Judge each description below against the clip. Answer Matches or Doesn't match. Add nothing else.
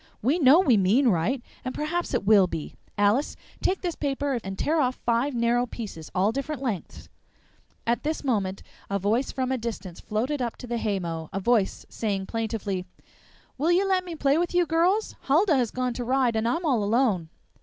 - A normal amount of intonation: Doesn't match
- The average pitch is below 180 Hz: Doesn't match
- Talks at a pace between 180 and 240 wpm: Matches